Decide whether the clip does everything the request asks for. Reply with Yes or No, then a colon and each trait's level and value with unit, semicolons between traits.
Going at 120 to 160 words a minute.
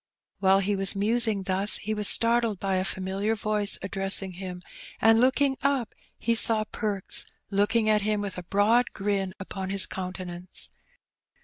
Yes: average, 155 wpm